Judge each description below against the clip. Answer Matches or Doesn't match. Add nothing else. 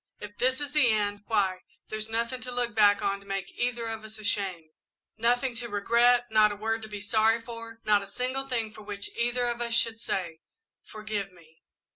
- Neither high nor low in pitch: Doesn't match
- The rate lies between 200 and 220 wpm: Matches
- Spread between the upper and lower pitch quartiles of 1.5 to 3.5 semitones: Matches